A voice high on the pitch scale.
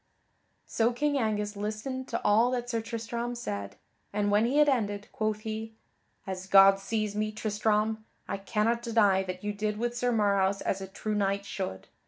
Yes: high, 215 Hz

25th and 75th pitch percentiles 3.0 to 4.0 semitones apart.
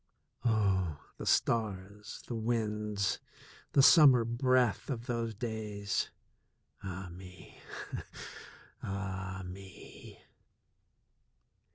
Yes: average, 3.4 semitones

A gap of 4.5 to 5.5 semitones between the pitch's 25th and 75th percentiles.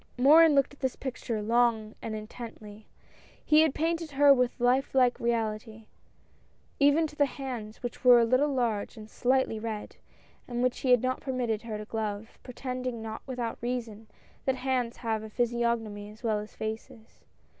No: average, 3.0 semitones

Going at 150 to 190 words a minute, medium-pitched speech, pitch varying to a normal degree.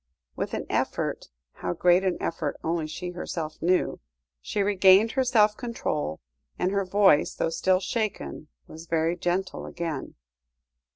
No: average, 140 wpm; medium, 180 Hz; average, 3.4 semitones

